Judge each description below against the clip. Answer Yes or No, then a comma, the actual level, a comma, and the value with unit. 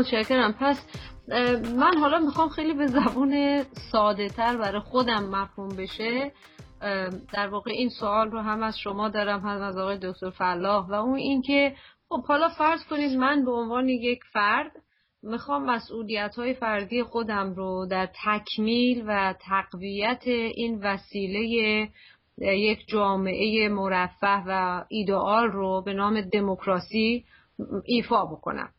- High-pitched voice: Yes, high, 215 Hz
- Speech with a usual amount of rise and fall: Yes, average, 3.7 semitones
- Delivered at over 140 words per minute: No, average, 135 wpm